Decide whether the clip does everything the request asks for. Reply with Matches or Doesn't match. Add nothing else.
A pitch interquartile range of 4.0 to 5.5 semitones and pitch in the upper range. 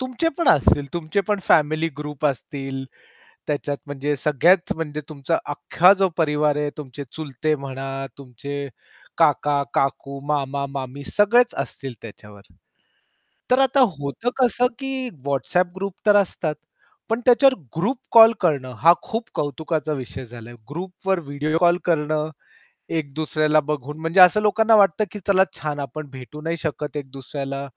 Doesn't match